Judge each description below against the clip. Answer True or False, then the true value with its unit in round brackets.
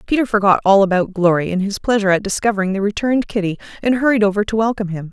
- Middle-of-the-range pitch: False (205 Hz)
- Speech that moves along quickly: True (225 wpm)